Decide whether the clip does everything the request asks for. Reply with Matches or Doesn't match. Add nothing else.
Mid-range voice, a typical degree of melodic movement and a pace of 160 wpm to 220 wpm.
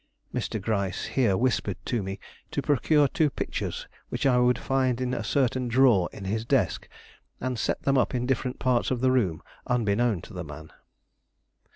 Doesn't match